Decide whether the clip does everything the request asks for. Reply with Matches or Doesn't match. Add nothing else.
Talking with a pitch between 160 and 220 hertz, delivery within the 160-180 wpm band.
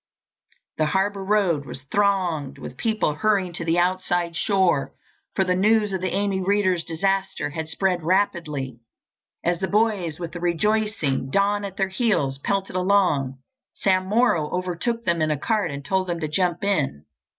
Matches